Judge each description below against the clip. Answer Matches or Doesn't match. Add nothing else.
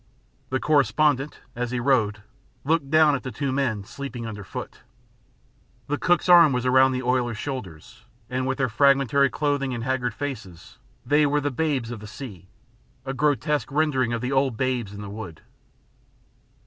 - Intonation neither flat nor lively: Matches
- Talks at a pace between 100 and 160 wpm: Doesn't match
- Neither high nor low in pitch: Doesn't match